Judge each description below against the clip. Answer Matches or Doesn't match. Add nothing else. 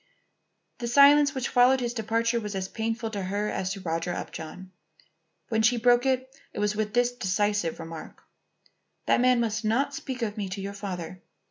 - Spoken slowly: Doesn't match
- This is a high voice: Matches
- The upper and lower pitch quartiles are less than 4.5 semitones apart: Matches